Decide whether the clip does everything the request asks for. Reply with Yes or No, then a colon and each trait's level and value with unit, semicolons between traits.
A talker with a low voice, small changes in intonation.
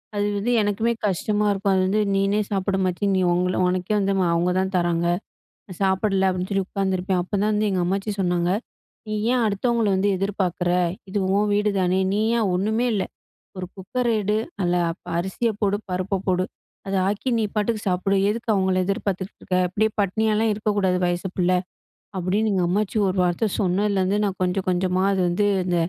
No: high, 195 Hz; narrow, 2.3 semitones